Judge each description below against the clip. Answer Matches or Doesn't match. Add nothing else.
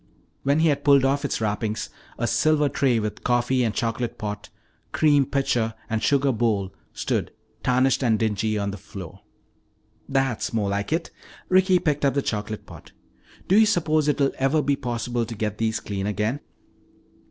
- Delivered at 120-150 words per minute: Doesn't match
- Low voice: Matches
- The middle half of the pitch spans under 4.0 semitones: Doesn't match